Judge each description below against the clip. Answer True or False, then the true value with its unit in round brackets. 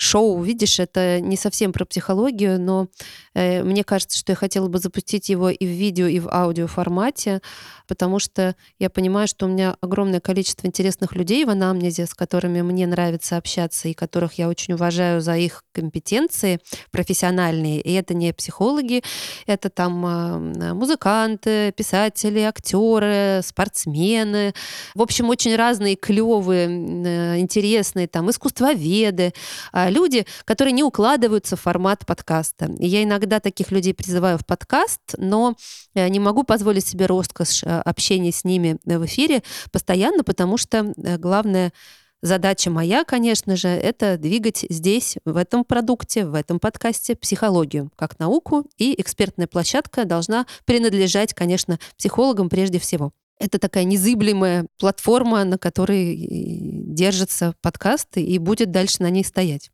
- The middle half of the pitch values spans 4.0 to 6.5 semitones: False (3.3 semitones)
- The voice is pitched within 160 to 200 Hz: True (190 Hz)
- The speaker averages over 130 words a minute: True (140 wpm)